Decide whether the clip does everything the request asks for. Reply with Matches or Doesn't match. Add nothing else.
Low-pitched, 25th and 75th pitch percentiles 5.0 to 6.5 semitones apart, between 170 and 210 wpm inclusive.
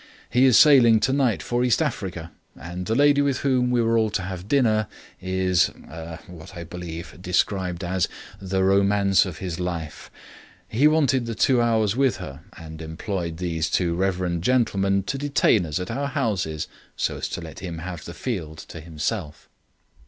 Matches